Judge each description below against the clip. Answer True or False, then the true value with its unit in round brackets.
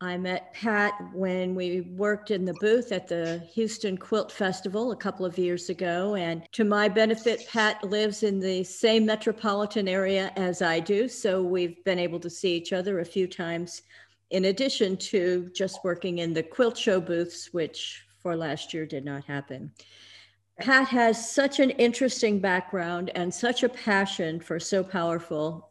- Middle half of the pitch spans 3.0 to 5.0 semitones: True (3.7 semitones)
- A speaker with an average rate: True (175 wpm)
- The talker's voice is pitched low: False (190 Hz)